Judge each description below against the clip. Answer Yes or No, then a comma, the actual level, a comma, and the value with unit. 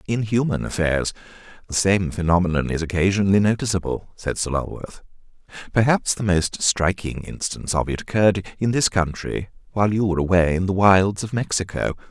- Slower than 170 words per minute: Yes, average, 160 wpm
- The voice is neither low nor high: No, very low, 95 Hz